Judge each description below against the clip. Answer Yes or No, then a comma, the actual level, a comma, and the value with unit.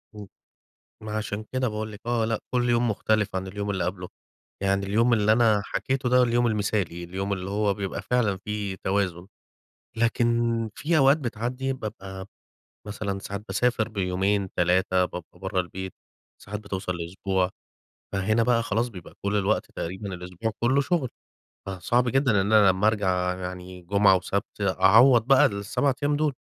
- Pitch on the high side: No, low, 105 Hz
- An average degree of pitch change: Yes, average, 3.6 semitones